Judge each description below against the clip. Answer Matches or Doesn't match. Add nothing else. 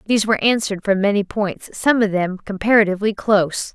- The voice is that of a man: Doesn't match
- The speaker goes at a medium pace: Matches